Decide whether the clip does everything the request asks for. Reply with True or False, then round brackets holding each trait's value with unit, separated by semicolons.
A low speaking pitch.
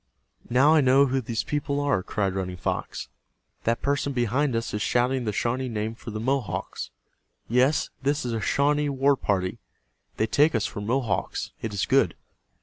True (125 Hz)